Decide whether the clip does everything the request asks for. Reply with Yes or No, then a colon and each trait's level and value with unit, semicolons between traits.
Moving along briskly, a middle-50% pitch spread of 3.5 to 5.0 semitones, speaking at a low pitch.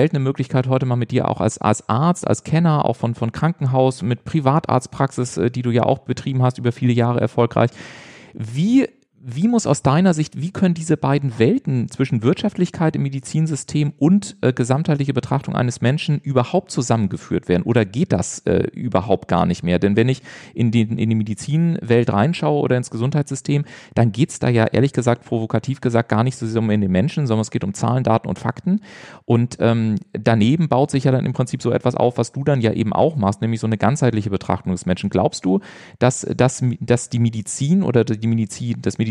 Yes: fast, 205 wpm; average, 4.0 semitones; low, 125 Hz